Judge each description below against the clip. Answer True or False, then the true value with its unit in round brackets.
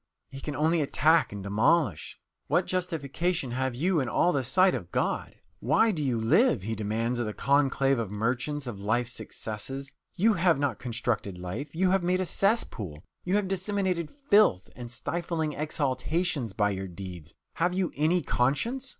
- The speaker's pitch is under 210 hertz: True (140 Hz)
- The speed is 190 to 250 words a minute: False (170 wpm)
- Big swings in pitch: True (7.4 semitones)